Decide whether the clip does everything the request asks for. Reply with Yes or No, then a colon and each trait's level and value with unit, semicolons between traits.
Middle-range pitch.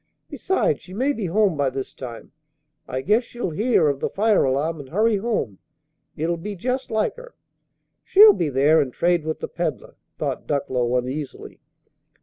Yes: medium, 165 Hz